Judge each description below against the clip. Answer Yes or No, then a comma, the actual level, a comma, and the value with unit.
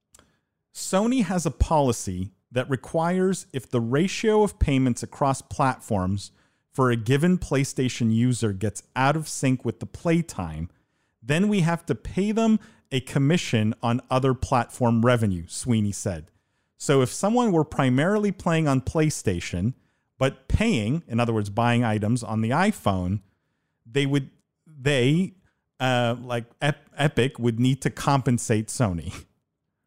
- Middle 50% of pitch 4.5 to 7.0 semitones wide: Yes, average, 5.0 semitones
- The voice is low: Yes, low, 130 Hz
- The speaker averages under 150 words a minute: Yes, average, 140 wpm